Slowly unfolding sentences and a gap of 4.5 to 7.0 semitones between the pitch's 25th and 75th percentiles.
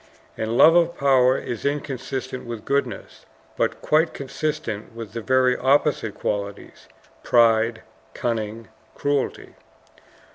No: slow, 110 wpm; average, 3.7 semitones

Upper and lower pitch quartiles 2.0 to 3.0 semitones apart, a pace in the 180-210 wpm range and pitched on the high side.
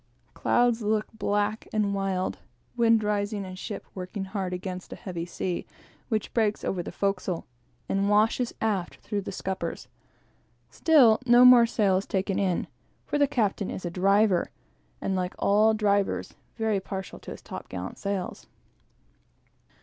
No: narrow, 2.6 semitones; average, 150 wpm; high, 200 Hz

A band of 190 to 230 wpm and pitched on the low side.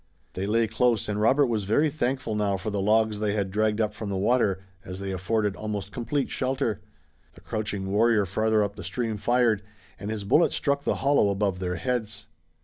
Yes: average, 200 wpm; low, 105 Hz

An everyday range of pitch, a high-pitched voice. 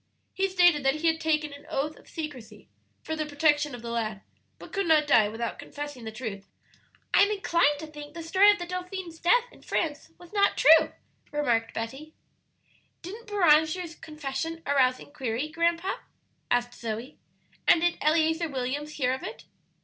Yes: average, 4.2 semitones; very high, 305 Hz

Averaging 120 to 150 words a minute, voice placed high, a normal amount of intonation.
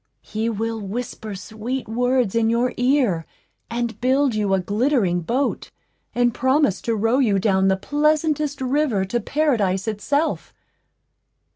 Yes: slow, 135 wpm; high, 235 Hz; average, 4.3 semitones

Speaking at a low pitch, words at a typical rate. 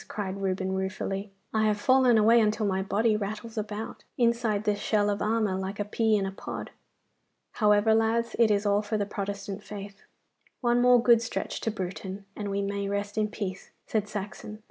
No: high, 210 Hz; average, 190 wpm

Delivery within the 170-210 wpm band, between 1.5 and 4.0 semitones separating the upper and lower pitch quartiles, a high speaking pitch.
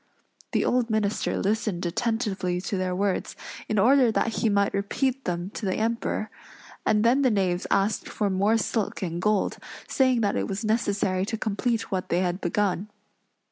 Yes: average, 175 wpm; average, 3.2 semitones; high, 205 Hz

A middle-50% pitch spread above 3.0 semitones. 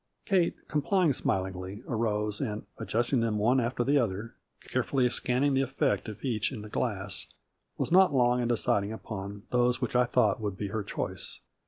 Yes: average, 3.7 semitones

